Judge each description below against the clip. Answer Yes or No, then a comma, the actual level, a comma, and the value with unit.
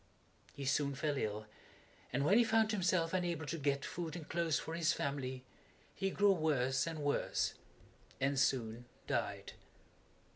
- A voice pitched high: No, medium, 150 Hz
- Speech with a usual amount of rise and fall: Yes, average, 4.0 semitones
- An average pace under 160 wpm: Yes, average, 150 wpm